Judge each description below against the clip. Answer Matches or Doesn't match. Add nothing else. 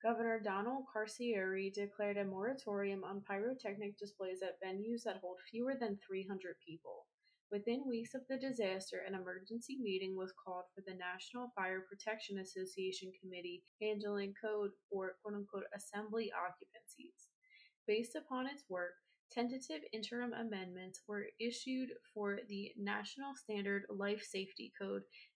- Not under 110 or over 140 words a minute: Matches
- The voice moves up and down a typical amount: Matches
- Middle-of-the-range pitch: Doesn't match